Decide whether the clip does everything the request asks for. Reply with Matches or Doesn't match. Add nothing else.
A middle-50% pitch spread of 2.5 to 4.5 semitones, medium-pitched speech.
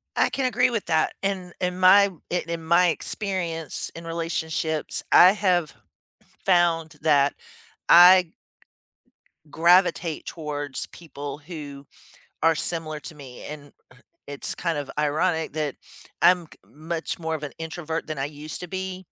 Matches